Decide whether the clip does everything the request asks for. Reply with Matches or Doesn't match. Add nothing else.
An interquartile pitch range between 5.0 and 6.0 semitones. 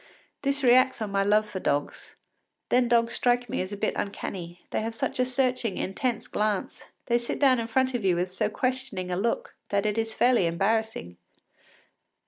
Doesn't match